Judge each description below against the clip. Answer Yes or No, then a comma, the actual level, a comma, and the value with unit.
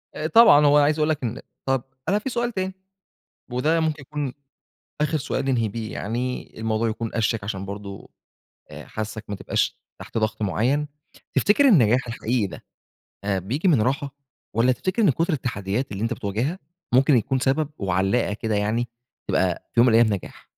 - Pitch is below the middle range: Yes, low, 125 Hz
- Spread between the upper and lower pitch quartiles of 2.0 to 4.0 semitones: No, wide, 5.4 semitones